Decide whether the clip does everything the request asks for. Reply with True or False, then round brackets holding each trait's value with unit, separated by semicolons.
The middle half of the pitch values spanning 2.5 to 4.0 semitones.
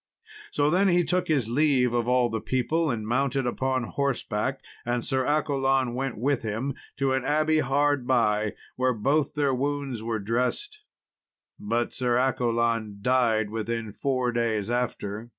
True (3.2 semitones)